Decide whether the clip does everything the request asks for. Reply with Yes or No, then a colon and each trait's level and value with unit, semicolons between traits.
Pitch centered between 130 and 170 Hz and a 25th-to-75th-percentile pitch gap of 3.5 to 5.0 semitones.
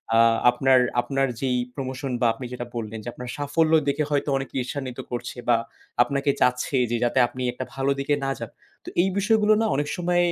No: low, 135 Hz; narrow, 2.5 semitones